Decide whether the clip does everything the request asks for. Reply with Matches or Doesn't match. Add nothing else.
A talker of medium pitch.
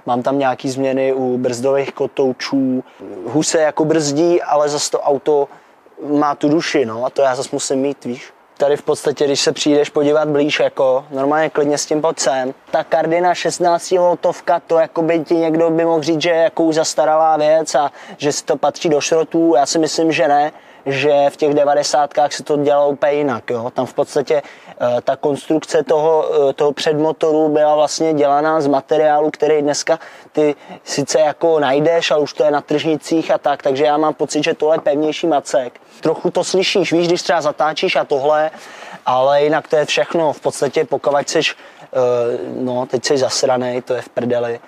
Matches